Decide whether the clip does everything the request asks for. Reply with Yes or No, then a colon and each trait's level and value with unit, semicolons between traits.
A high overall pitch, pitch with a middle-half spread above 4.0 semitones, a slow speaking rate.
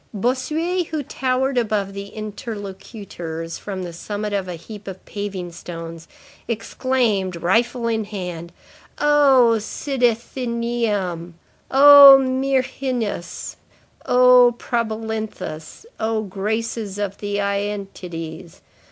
Yes: high, 215 Hz; average, 4.5 semitones; slow, 95 wpm